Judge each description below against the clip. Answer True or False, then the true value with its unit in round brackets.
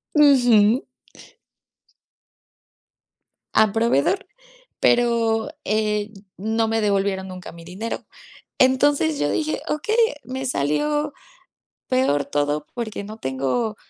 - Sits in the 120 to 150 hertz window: False (220 Hz)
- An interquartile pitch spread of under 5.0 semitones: False (5.6 semitones)